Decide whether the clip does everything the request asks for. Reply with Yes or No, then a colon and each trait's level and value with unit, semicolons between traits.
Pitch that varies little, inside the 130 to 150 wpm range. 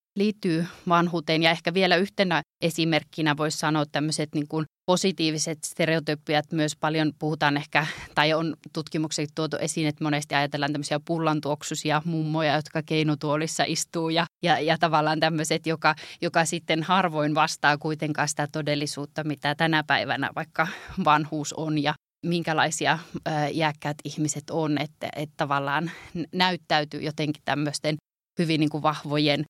Yes: narrow, 1.5 semitones; average, 140 wpm